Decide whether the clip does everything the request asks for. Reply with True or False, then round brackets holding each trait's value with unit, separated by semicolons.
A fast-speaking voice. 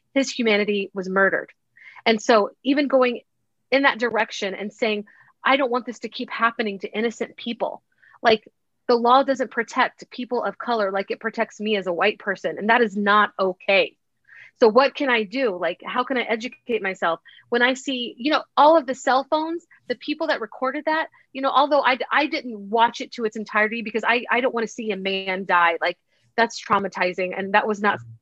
True (210 wpm)